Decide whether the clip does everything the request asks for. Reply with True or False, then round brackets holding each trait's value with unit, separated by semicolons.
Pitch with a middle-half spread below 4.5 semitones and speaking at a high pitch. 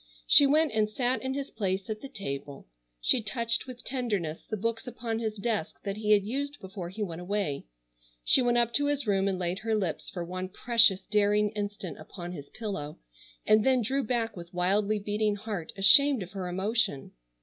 True (3.8 semitones; 210 Hz)